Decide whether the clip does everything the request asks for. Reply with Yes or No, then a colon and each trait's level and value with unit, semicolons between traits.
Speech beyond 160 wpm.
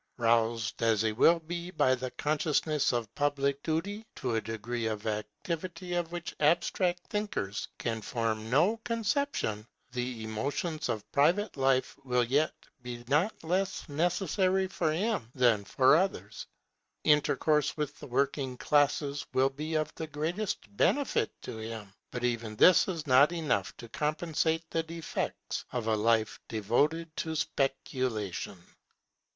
No: average, 140 wpm